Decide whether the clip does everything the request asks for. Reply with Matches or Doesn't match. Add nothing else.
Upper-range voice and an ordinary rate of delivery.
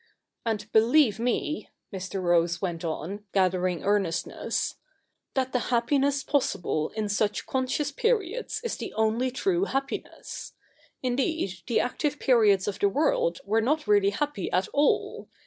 Matches